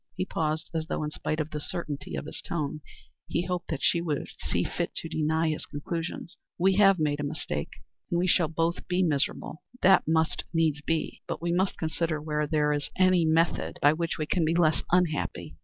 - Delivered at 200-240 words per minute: Yes, fast, 205 wpm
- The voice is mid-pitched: Yes, medium, 160 Hz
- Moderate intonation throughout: No, narrow, 2.2 semitones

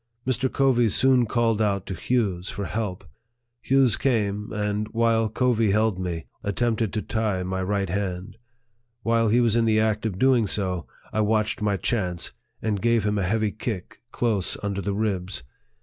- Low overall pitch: Yes, low, 105 Hz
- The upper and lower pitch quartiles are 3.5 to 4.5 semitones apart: No, narrow, 2.6 semitones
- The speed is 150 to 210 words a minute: Yes, average, 175 wpm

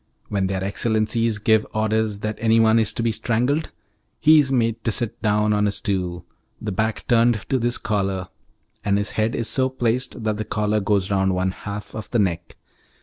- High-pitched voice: No, low, 110 Hz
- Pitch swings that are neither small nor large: No, narrow, 2.3 semitones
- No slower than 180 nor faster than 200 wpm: Yes, average, 195 wpm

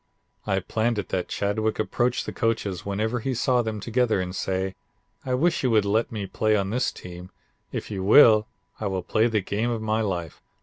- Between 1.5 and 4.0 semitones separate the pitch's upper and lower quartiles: Yes, average, 3.0 semitones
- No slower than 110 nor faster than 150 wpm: No, fast, 205 wpm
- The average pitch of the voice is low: Yes, low, 110 Hz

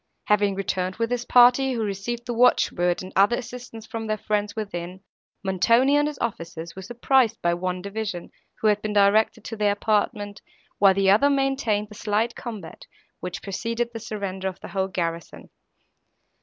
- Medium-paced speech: Yes, average, 175 wpm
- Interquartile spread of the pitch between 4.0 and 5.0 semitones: No, average, 3.5 semitones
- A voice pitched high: Yes, high, 210 Hz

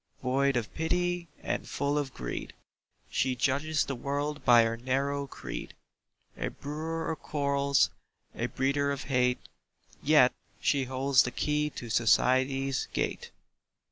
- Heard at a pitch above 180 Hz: No, medium, 140 Hz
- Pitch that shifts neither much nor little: No, narrow, 2.3 semitones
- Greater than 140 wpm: No, slow, 135 wpm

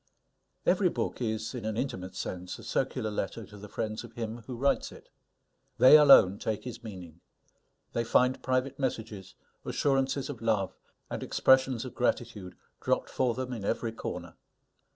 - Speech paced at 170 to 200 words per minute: No, average, 160 wpm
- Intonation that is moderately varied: Yes, average, 3.7 semitones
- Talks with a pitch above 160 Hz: No, low, 115 Hz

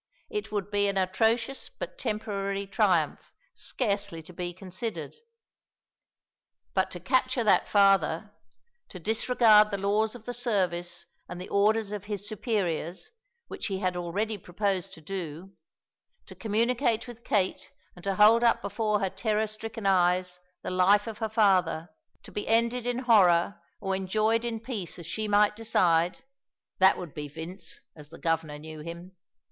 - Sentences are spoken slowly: No, average, 155 wpm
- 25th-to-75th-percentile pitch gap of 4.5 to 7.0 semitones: No, average, 3.5 semitones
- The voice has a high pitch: Yes, high, 200 Hz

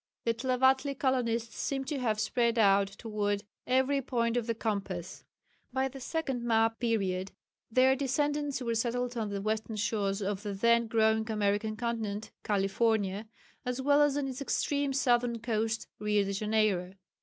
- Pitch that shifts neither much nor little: Yes, average, 3.5 semitones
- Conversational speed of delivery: Yes, average, 155 wpm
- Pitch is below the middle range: No, high, 230 Hz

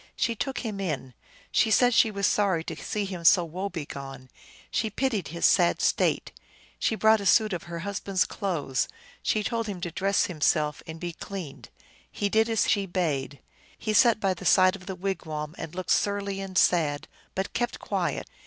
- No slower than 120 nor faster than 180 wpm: No, average, 190 wpm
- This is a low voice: No, high, 190 Hz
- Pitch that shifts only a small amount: No, average, 3.8 semitones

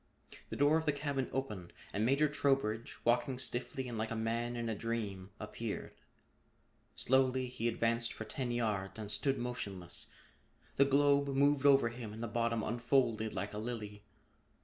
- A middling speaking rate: Yes, average, 165 wpm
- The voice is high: No, low, 120 Hz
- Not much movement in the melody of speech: No, average, 3.5 semitones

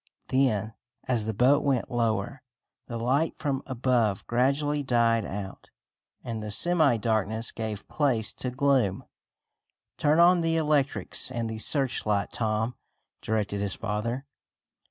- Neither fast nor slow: No, slow, 130 wpm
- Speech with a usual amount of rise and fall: Yes, average, 4.1 semitones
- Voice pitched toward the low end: Yes, low, 120 Hz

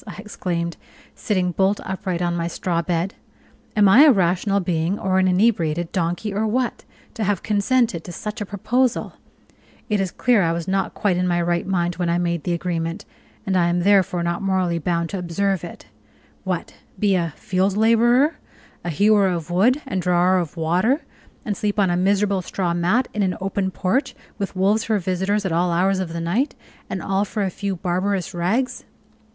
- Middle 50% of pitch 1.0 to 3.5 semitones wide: Yes, average, 2.9 semitones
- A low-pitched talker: No, high, 190 Hz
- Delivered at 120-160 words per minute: No, average, 195 wpm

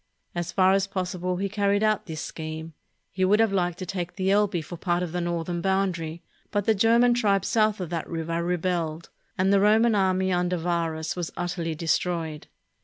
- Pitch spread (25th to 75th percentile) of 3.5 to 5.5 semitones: No, narrow, 2.6 semitones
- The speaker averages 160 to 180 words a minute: No, average, 190 wpm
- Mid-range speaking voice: Yes, medium, 180 Hz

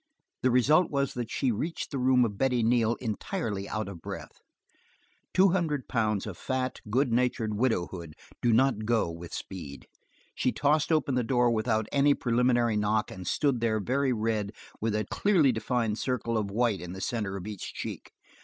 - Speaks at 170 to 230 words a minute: Yes, average, 180 wpm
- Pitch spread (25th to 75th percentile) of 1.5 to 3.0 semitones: No, average, 3.5 semitones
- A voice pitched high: No, low, 115 Hz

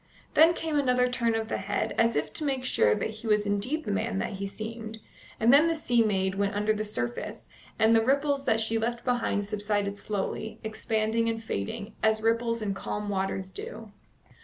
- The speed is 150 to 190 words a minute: No, average, 200 wpm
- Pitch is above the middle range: Yes, high, 220 Hz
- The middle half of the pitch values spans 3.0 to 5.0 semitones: No, narrow, 2.5 semitones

